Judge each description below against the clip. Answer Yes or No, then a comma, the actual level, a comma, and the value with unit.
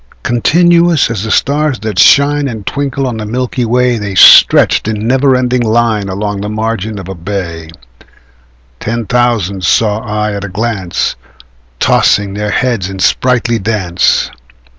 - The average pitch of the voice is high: No, low, 110 Hz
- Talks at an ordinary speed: Yes, average, 150 wpm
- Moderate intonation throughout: Yes, average, 3.7 semitones